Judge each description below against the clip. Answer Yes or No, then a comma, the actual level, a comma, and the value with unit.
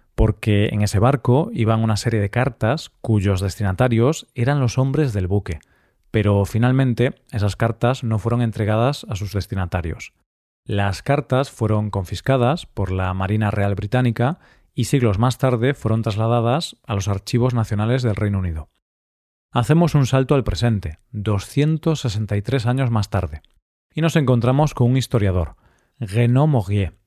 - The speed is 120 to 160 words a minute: Yes, average, 145 wpm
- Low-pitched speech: Yes, low, 115 Hz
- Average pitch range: Yes, average, 4.1 semitones